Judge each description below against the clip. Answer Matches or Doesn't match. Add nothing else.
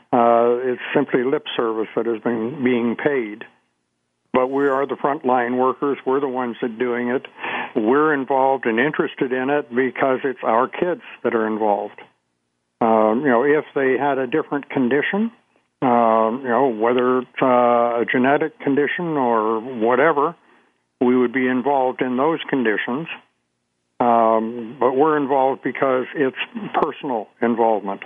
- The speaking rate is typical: Matches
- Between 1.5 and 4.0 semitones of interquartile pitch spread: Matches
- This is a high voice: Doesn't match